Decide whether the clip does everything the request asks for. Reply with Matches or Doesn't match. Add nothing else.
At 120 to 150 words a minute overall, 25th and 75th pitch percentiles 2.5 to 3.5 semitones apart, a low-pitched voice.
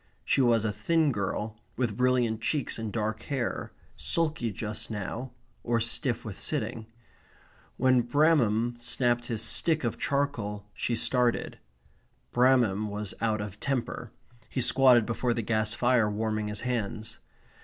Matches